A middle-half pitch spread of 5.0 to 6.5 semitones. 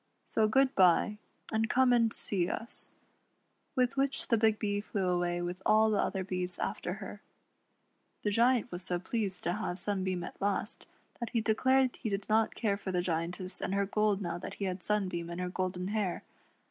No: average, 3.4 semitones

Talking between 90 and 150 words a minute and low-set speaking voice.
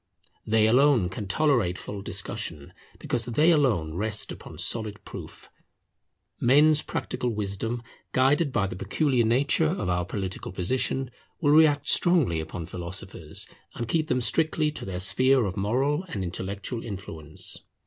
Yes: average, 140 wpm; low, 115 Hz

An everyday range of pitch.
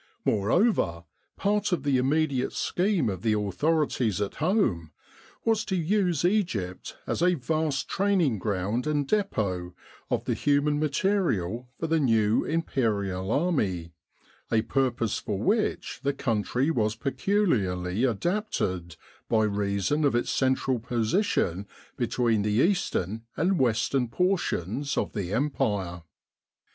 No: wide, 8.0 semitones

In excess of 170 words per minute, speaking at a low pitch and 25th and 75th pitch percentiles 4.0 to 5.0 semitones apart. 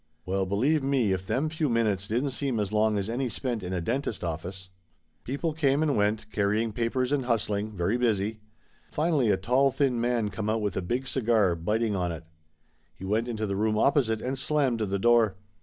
Yes: average, 200 wpm; low, 110 Hz; average, 4.3 semitones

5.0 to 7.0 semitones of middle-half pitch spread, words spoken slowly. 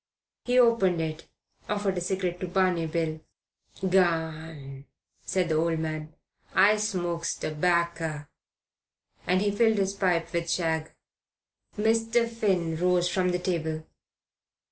No: average, 3.0 semitones; slow, 120 wpm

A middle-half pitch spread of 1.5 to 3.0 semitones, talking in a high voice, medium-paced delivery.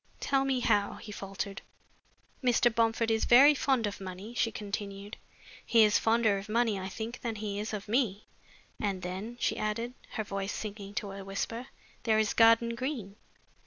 Yes: average, 2.7 semitones; high, 215 Hz; average, 175 wpm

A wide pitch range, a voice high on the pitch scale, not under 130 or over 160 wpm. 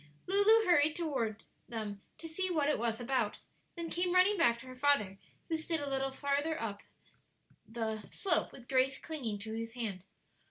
No: wide, 6.2 semitones; very high, 270 Hz; average, 175 wpm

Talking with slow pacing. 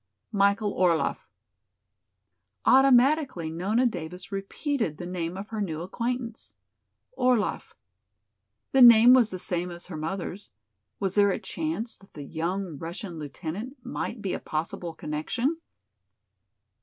Yes: slow, 125 wpm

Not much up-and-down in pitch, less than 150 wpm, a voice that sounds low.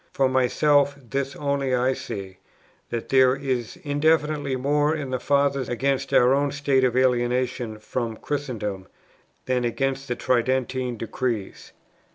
Yes: narrow, 2.3 semitones; slow, 135 wpm; low, 130 Hz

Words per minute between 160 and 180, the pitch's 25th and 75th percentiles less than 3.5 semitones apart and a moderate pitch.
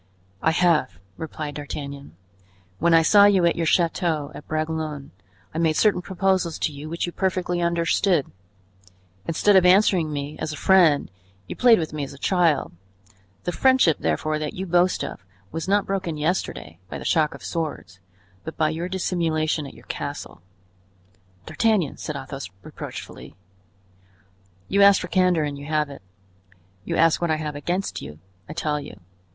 Yes: average, 170 wpm; average, 3.1 semitones; medium, 160 Hz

